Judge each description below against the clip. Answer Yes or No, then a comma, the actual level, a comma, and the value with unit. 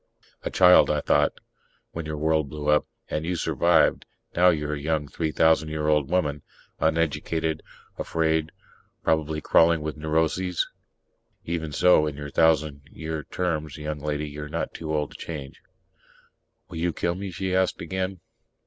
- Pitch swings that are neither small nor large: No, narrow, 1.8 semitones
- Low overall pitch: Yes, very low, 80 Hz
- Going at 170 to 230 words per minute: No, average, 155 wpm